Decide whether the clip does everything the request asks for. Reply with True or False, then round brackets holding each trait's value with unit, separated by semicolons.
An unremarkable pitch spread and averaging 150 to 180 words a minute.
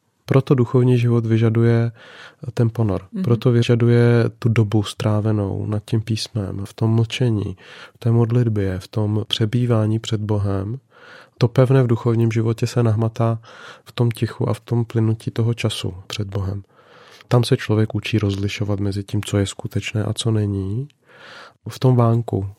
False (2.1 semitones; 155 wpm)